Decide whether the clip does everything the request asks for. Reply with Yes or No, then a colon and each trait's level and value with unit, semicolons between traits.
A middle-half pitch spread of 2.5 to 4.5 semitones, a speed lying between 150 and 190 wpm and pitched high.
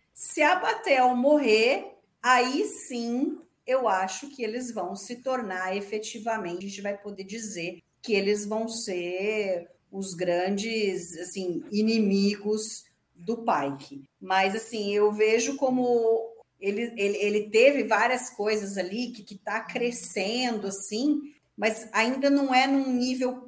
No: average, 4.1 semitones; average, 135 wpm; high, 220 Hz